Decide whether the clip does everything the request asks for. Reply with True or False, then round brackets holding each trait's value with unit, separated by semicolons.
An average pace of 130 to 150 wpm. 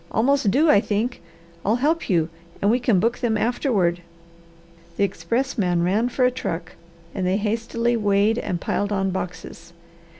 False (160 wpm)